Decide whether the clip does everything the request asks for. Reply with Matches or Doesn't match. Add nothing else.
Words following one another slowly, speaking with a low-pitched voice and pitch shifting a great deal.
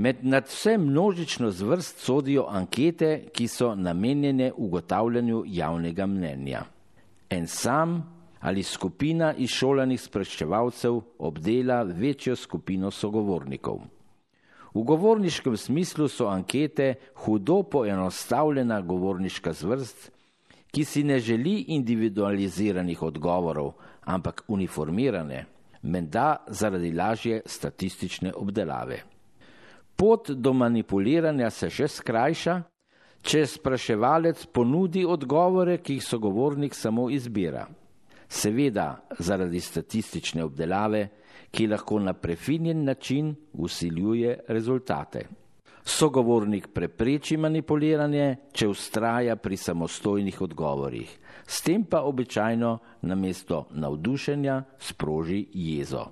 Matches